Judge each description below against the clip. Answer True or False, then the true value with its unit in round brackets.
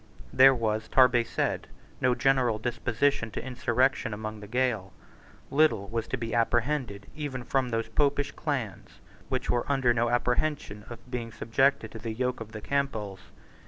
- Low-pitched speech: True (120 Hz)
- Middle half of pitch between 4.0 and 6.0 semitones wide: False (3.1 semitones)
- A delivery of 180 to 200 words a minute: False (160 wpm)